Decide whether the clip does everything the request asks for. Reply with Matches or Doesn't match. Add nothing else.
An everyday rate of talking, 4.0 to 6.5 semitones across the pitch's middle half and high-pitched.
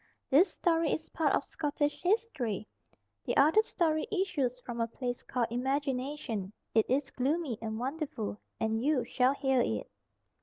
Matches